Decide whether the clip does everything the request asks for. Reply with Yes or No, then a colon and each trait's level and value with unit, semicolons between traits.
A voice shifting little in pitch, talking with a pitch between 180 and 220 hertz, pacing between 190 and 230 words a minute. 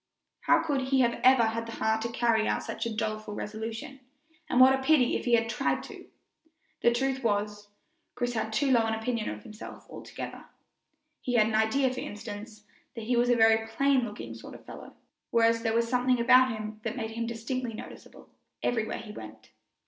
No: narrow, 2.2 semitones; high, 230 Hz; average, 200 wpm